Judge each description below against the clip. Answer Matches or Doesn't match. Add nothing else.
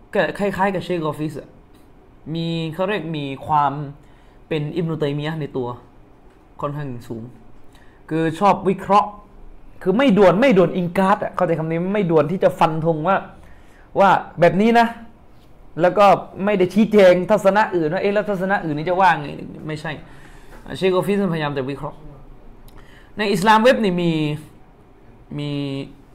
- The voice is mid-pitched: Matches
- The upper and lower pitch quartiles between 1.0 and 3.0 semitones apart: Doesn't match